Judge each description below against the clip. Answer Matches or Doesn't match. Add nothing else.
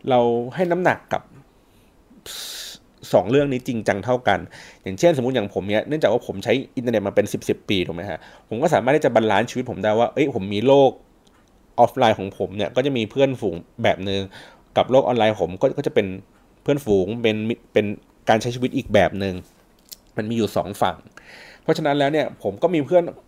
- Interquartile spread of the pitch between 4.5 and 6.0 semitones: Matches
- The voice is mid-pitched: Doesn't match